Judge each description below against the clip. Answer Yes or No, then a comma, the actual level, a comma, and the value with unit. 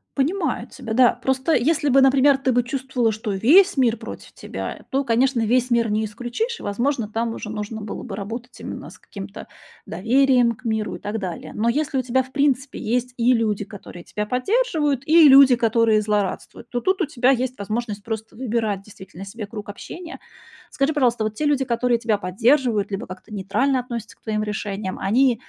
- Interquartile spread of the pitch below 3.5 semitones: No, average, 3.8 semitones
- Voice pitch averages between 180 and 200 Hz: No, high, 235 Hz